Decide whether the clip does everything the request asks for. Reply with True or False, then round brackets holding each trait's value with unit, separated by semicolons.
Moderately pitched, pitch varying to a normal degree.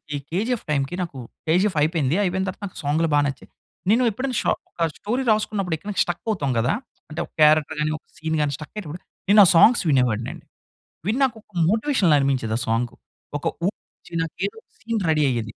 False (165 Hz; 6.2 semitones)